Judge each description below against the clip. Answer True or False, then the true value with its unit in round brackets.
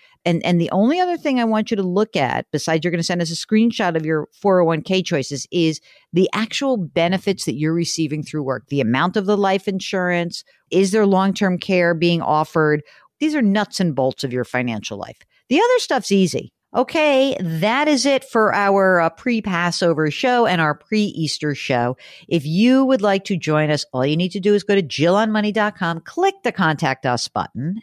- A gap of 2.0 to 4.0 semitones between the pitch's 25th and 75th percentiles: False (5.2 semitones)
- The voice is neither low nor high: True (180 Hz)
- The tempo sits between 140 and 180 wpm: False (205 wpm)